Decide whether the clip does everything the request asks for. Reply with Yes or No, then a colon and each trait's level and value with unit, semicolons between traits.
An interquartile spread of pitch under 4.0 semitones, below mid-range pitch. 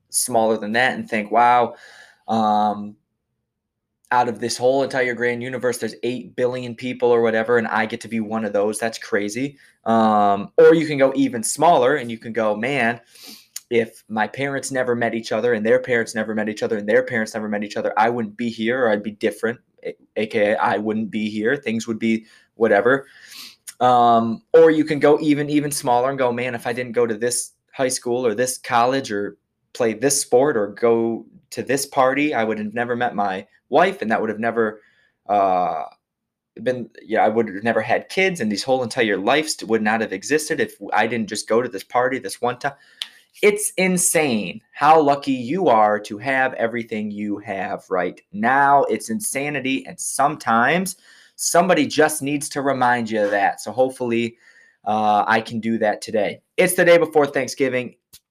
Yes: average, 3.6 semitones; low, 120 Hz